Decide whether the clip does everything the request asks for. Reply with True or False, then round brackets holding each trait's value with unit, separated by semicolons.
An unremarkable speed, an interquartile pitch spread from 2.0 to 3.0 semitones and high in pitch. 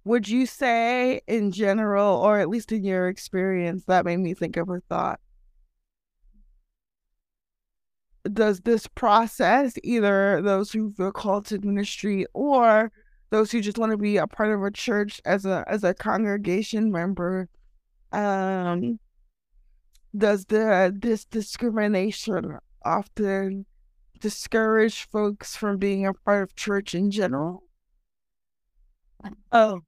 False (125 wpm; 2.5 semitones; 205 Hz)